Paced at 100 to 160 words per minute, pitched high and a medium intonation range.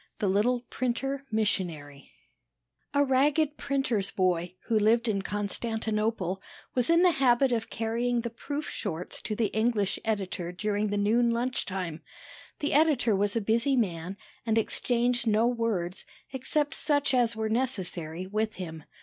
Yes: average, 150 wpm; high, 225 Hz; average, 4.0 semitones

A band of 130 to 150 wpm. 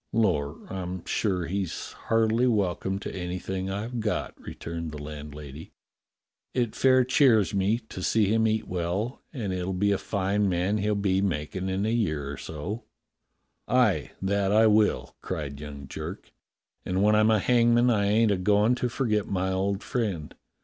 No: average, 170 wpm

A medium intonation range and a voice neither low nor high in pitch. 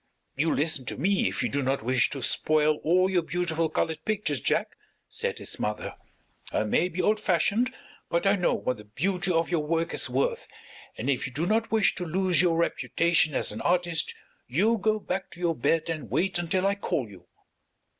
Yes: average, 4.0 semitones; medium, 170 Hz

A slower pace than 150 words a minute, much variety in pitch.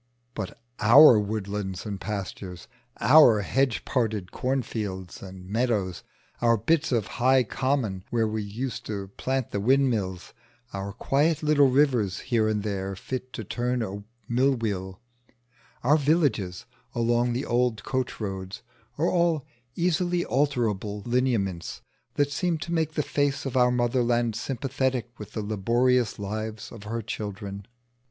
No: average, 140 wpm; average, 4.5 semitones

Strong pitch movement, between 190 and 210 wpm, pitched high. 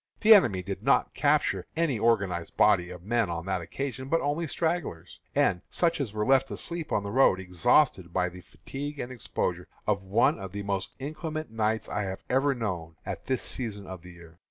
No: wide, 7.0 semitones; average, 200 wpm; low, 110 Hz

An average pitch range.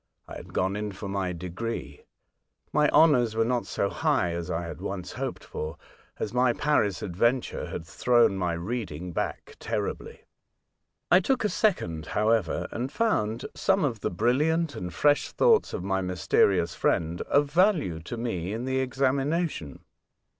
No: wide, 7.7 semitones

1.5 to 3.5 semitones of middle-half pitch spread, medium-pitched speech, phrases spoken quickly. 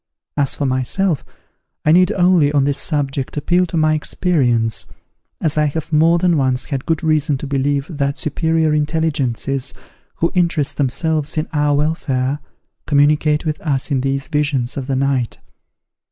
No: average, 2.7 semitones; medium, 150 Hz; average, 155 wpm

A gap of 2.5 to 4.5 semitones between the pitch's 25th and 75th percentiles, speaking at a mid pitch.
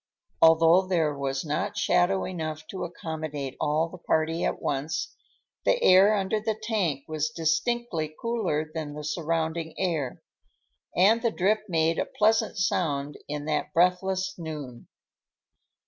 Yes: average, 3.6 semitones; medium, 165 Hz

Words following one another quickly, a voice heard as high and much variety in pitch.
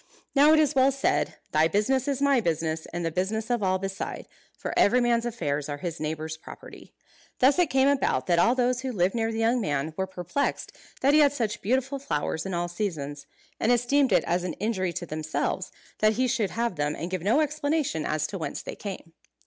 Yes: fast, 215 wpm; high, 210 Hz; wide, 7.5 semitones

